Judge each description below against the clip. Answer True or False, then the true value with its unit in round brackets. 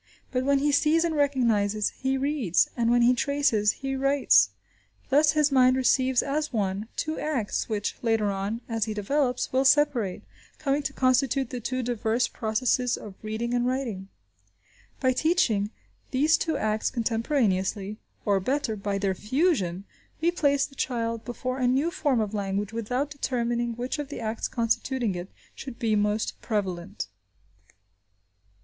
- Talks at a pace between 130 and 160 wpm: True (155 wpm)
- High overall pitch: True (245 Hz)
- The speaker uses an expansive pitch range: False (4.3 semitones)